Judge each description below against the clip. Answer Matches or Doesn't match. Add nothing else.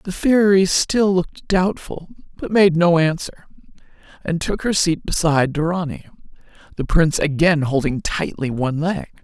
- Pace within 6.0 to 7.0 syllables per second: Doesn't match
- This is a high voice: Doesn't match